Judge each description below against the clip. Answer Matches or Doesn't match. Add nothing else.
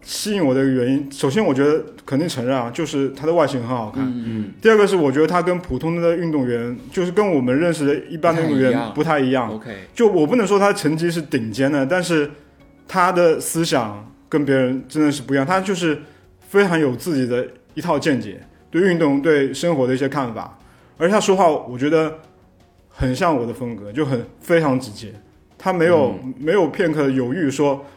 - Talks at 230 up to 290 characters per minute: Doesn't match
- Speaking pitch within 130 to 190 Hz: Matches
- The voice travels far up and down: Doesn't match